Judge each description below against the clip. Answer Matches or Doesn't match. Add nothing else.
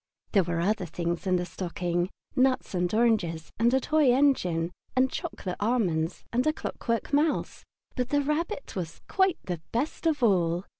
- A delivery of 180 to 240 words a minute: Doesn't match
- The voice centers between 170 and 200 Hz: Doesn't match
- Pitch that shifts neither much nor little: Doesn't match